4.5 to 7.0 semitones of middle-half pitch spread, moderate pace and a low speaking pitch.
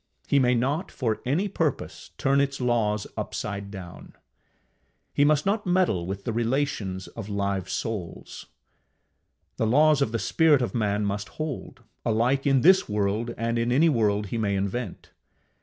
Yes: wide, 5.4 semitones; average, 155 wpm; low, 115 Hz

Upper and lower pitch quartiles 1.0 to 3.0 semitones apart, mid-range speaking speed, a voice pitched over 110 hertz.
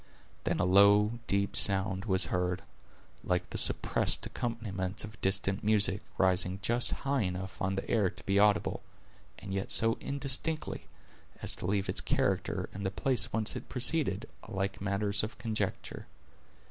No: narrow, 2.5 semitones; average, 155 wpm; low, 100 Hz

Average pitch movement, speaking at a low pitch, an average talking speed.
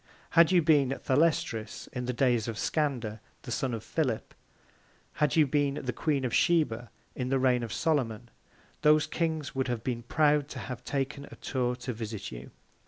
Yes: average, 4.0 semitones; low, 130 Hz; average, 180 wpm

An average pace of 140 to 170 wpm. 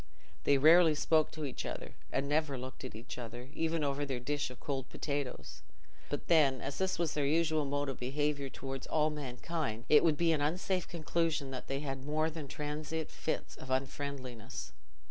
No: average, 185 wpm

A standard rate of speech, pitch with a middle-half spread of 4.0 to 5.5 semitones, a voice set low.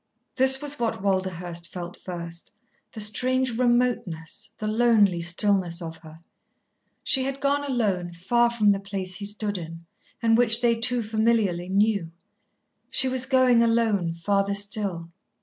No: average, 145 wpm; average, 5.1 semitones; high, 210 Hz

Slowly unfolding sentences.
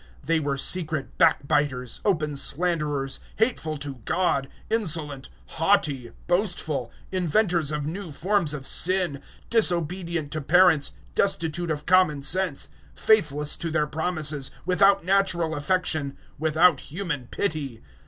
Yes: slow, 125 wpm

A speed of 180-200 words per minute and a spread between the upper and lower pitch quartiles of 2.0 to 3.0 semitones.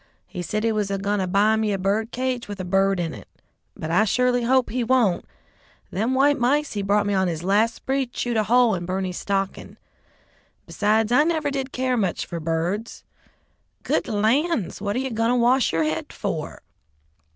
No: average, 195 wpm; average, 4.4 semitones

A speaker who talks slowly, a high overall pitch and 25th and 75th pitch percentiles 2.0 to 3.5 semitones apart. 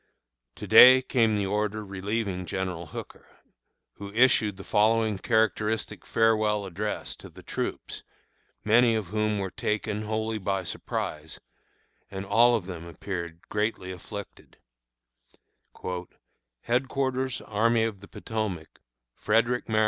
No: slow, 120 wpm; low, 105 Hz; average, 2.7 semitones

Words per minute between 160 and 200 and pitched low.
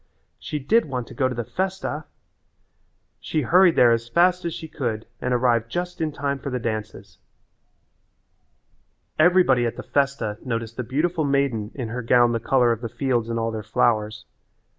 Yes: average, 180 wpm; low, 125 Hz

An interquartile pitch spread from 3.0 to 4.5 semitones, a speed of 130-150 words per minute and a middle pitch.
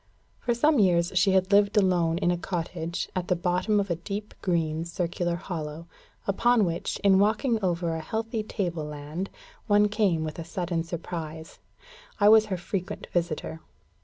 No: average, 3.4 semitones; average, 165 wpm; medium, 180 Hz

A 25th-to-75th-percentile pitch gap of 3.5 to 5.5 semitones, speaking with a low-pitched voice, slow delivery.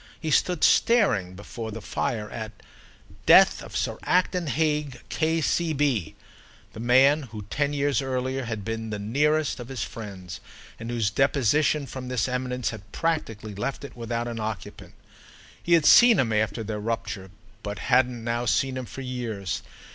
No: average, 4.5 semitones; low, 125 Hz; average, 160 wpm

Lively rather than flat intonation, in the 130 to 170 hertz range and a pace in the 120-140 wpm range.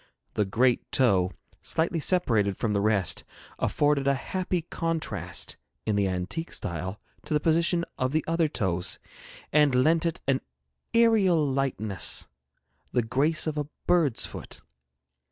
Yes: wide, 7.7 semitones; medium, 140 Hz; slow, 135 wpm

